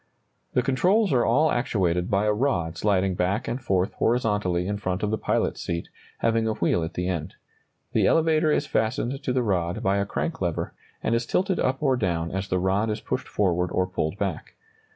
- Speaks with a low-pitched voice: Yes, low, 105 Hz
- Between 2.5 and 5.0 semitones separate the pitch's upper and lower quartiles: No, wide, 5.4 semitones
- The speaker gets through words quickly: Yes, fast, 210 wpm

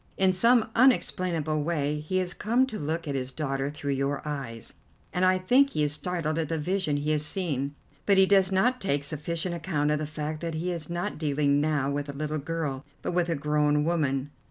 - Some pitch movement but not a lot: Yes, average, 3.8 semitones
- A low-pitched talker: No, medium, 155 Hz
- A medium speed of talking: No, fast, 215 wpm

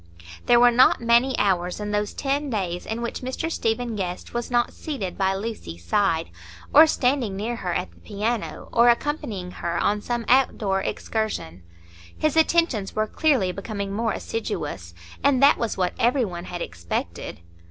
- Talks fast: No, average, 165 wpm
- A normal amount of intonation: Yes, average, 4.4 semitones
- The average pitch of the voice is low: No, high, 220 Hz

